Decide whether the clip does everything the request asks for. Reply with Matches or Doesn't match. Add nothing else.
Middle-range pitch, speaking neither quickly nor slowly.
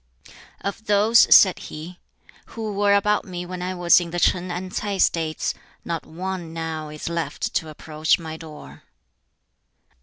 Matches